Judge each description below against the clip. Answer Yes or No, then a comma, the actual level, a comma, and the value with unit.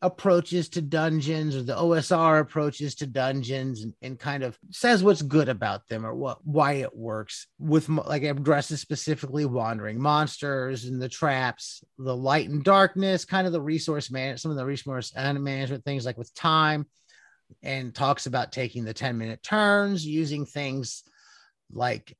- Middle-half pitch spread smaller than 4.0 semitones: Yes, average, 3.3 semitones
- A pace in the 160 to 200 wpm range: Yes, average, 170 wpm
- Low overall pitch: No, medium, 145 Hz